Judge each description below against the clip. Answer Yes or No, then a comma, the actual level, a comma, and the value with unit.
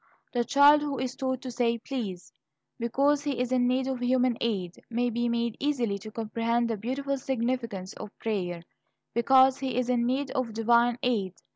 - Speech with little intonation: Yes, narrow, 2.2 semitones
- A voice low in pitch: No, high, 245 Hz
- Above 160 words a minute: Yes, average, 180 wpm